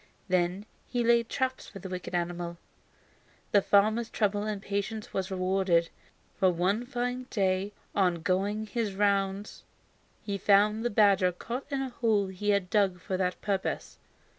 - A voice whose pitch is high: Yes, high, 200 Hz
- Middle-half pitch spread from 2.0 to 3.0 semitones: Yes, narrow, 2.6 semitones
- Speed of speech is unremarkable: Yes, average, 155 wpm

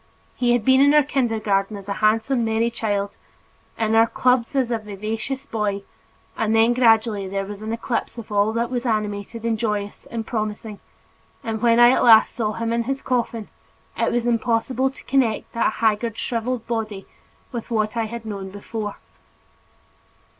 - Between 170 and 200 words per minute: Yes, average, 175 wpm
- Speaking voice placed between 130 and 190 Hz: No, high, 225 Hz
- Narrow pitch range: Yes, narrow, 2.1 semitones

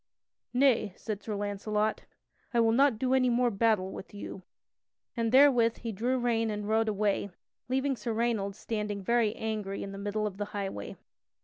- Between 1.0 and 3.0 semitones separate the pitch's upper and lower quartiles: Yes, average, 2.7 semitones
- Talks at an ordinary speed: Yes, average, 175 wpm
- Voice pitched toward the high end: Yes, high, 220 Hz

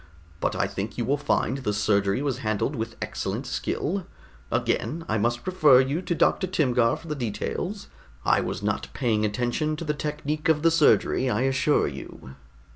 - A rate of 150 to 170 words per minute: No, average, 180 wpm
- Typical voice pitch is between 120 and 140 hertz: Yes, low, 135 Hz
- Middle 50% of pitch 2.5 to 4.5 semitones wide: No, average, 4.9 semitones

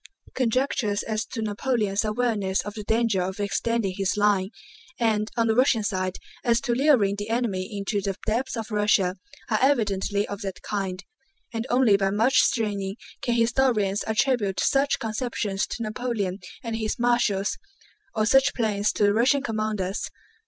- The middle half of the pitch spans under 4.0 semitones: Yes, average, 2.8 semitones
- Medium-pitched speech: No, high, 215 Hz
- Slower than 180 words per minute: Yes, average, 160 wpm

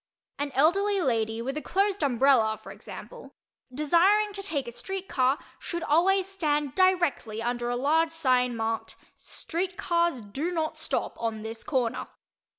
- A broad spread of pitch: Yes, wide, 6.8 semitones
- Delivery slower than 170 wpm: Yes, average, 155 wpm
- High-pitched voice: Yes, very high, 295 Hz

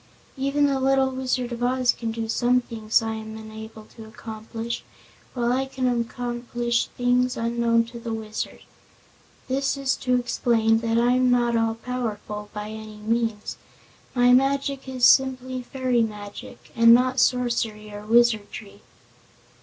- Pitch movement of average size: No, narrow, 2.2 semitones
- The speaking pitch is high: Yes, high, 235 Hz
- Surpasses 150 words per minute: No, average, 145 wpm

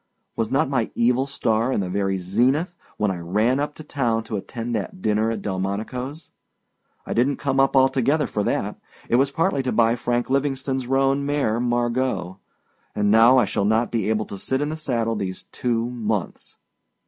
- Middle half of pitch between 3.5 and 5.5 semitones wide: Yes, average, 3.8 semitones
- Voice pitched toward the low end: Yes, low, 120 Hz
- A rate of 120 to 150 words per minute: No, average, 185 wpm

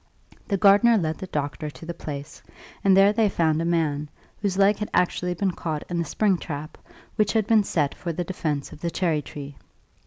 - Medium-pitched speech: Yes, medium, 170 Hz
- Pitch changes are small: No, average, 4.4 semitones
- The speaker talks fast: Yes, fast, 210 wpm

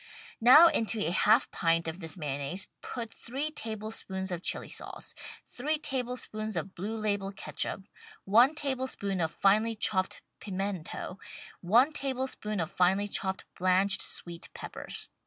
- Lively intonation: No, average, 4.3 semitones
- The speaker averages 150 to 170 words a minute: No, average, 140 wpm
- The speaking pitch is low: No, high, 205 Hz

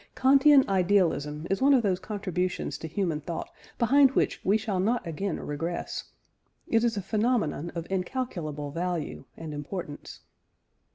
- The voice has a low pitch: No, medium, 185 Hz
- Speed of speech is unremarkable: Yes, average, 145 wpm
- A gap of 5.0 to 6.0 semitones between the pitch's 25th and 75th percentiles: Yes, wide, 5.6 semitones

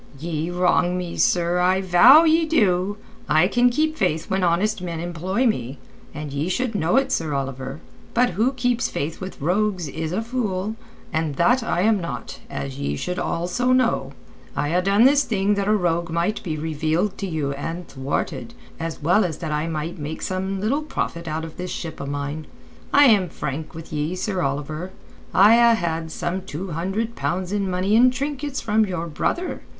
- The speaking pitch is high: No, medium, 180 Hz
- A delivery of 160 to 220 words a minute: Yes, average, 190 wpm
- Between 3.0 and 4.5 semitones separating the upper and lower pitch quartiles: No, average, 5.1 semitones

